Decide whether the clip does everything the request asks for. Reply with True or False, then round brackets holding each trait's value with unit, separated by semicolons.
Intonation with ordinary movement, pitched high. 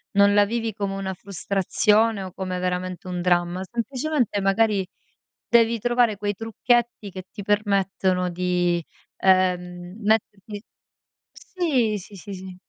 True (3.3 semitones; 200 Hz)